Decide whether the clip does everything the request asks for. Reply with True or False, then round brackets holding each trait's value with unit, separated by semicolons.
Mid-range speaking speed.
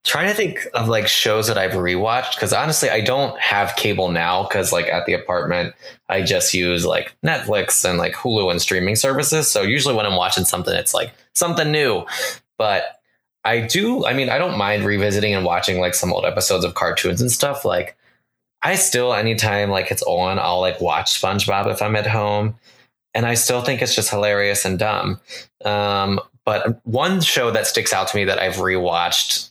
True (195 wpm)